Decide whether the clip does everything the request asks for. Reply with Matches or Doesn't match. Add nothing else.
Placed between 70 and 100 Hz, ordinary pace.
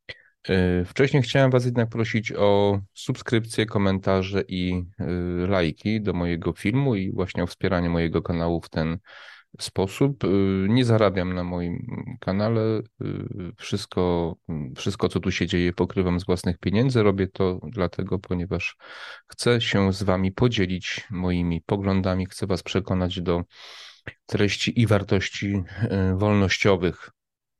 Matches